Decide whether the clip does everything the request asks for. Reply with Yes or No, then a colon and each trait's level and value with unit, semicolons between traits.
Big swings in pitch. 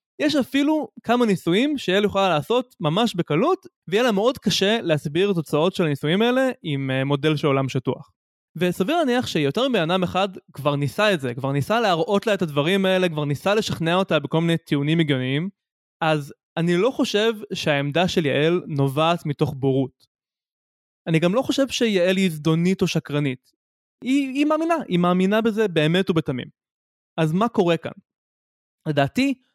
Yes: wide, 6.2 semitones